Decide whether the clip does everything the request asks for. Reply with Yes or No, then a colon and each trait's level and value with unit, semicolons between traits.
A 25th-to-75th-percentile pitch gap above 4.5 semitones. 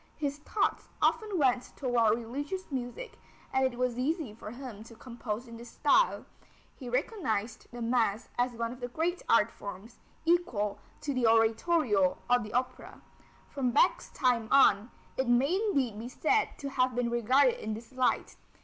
No: average, 3.5 semitones